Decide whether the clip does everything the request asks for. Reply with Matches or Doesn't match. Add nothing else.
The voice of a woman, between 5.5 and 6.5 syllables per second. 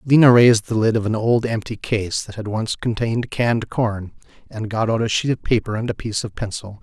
Doesn't match